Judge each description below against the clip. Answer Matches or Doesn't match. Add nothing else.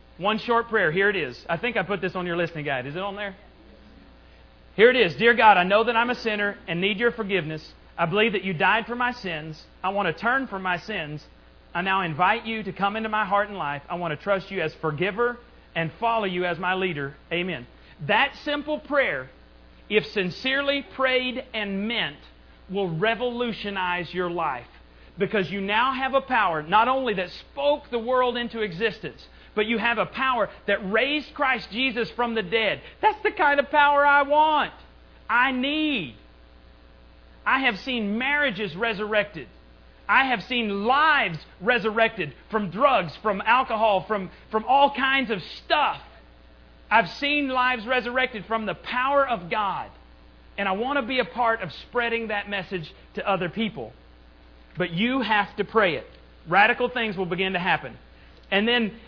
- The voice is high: Matches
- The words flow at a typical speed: Matches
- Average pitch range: Doesn't match